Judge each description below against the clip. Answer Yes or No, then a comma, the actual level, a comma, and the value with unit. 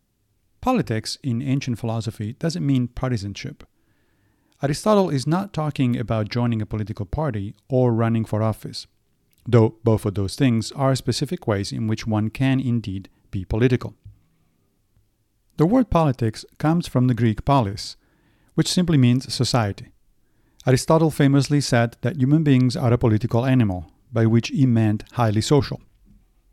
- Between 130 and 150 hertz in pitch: No, low, 120 Hz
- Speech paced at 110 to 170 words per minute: Yes, average, 145 wpm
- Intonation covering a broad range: No, average, 4.0 semitones